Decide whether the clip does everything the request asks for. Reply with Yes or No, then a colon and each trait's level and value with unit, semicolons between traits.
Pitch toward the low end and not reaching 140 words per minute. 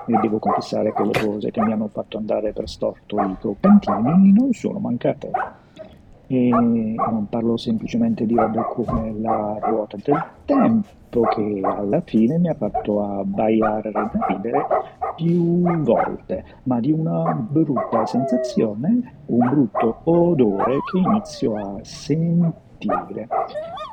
No: medium, 145 Hz; average, 130 wpm